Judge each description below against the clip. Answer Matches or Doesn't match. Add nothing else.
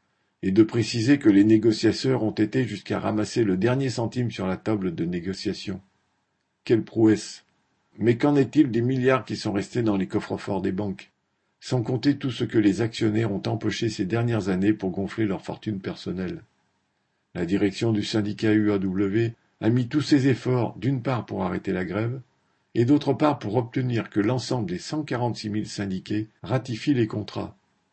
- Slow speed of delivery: Doesn't match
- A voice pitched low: Matches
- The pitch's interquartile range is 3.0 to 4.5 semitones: Matches